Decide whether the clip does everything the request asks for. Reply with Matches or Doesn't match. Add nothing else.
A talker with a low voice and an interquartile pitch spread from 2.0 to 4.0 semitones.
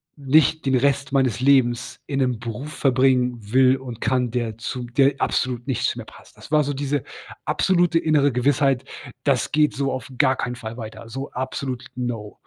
Matches